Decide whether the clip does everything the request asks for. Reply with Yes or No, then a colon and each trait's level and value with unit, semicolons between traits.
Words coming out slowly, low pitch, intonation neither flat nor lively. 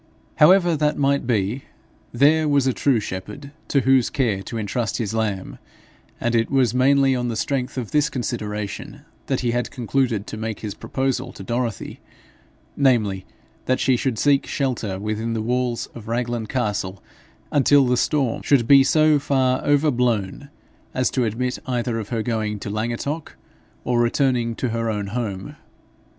No: average, 165 wpm; low, 120 Hz; average, 3.6 semitones